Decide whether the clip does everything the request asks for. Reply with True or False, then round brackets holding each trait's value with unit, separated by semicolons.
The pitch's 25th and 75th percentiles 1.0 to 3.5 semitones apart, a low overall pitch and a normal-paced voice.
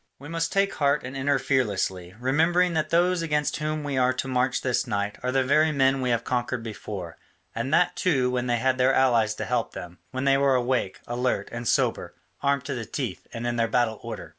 False (3.0 semitones; 130 Hz; 220 wpm)